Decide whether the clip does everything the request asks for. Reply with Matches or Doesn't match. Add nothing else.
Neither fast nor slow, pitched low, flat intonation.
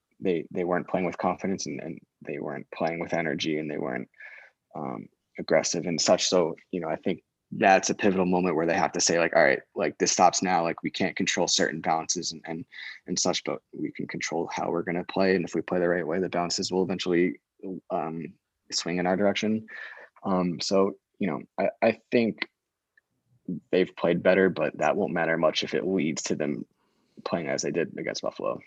Doesn't match